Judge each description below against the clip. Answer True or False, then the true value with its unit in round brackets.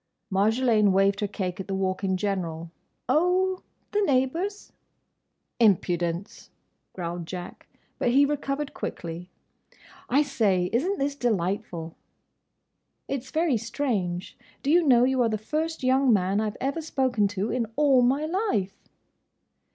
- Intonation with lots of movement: True (6.6 semitones)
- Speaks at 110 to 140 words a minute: True (135 wpm)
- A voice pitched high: True (230 Hz)